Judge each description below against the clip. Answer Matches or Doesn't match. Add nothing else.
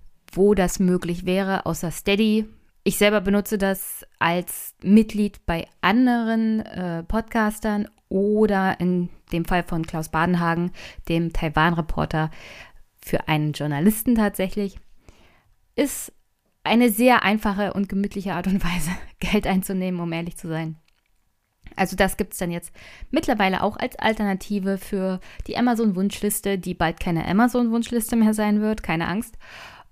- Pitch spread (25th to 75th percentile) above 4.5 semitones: Doesn't match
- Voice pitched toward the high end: Matches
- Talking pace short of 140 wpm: Matches